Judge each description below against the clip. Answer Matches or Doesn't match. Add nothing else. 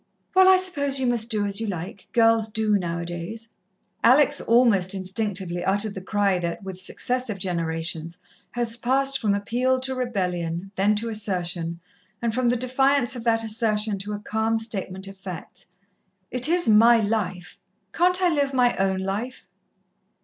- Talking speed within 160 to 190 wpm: Matches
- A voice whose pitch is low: Doesn't match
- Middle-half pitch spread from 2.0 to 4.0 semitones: Doesn't match